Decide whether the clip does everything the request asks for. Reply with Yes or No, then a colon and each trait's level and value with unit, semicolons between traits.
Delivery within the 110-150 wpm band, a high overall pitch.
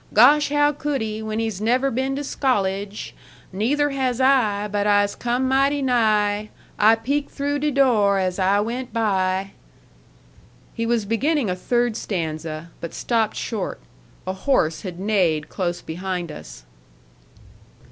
Yes: average, 145 wpm; high, 220 Hz